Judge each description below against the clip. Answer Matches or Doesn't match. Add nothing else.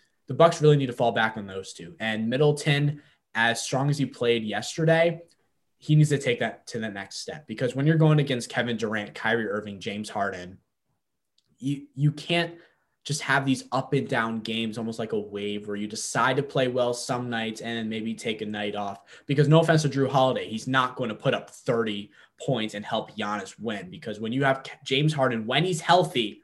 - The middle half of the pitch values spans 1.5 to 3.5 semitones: Doesn't match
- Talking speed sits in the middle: Doesn't match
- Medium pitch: Doesn't match